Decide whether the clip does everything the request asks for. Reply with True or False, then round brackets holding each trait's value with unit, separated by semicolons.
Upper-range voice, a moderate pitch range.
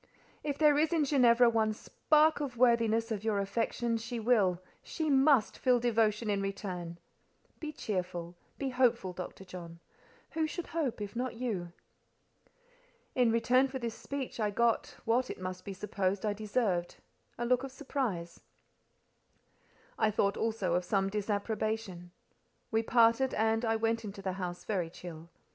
True (225 Hz; 4.2 semitones)